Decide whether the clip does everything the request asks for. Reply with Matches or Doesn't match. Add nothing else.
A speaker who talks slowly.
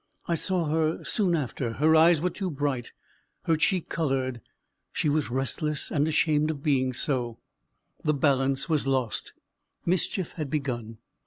Doesn't match